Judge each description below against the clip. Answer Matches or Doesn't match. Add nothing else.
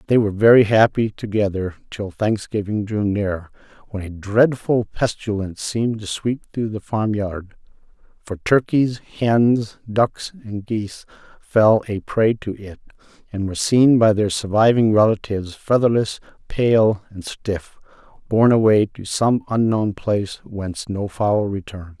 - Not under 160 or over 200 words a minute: Doesn't match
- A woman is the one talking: Doesn't match